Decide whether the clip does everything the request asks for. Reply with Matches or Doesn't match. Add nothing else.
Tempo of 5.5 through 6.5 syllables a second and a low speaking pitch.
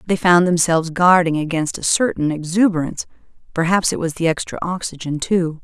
Doesn't match